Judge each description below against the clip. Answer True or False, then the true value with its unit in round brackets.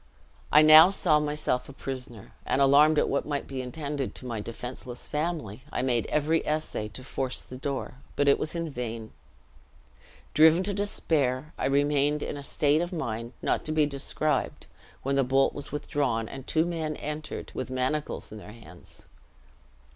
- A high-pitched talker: False (140 Hz)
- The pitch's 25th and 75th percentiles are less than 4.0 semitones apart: True (3.3 semitones)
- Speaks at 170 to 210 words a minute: True (175 wpm)